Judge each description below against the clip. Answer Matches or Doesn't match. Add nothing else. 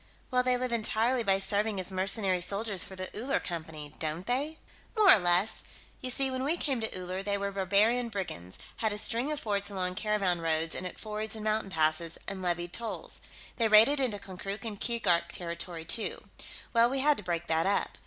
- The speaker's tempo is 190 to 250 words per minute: Matches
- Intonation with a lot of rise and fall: Doesn't match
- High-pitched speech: Matches